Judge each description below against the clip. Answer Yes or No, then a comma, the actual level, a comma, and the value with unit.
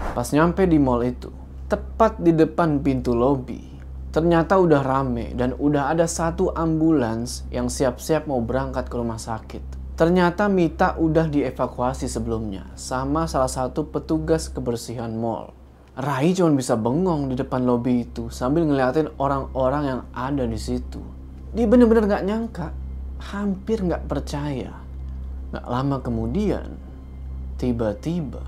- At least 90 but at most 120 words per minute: No, average, 130 wpm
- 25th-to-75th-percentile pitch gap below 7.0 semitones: No, wide, 8.7 semitones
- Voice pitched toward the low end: Yes, low, 130 Hz